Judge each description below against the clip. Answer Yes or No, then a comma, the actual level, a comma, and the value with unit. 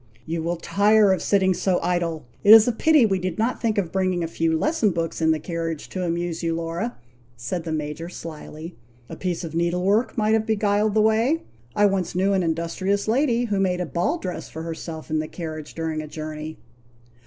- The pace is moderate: No, fast, 215 wpm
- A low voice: No, medium, 180 Hz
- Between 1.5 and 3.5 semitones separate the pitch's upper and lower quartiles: No, average, 4.0 semitones